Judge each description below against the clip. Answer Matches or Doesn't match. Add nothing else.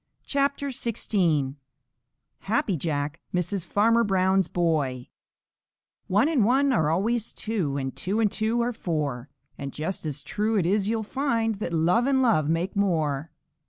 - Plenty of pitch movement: Matches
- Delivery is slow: Doesn't match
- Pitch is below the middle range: Doesn't match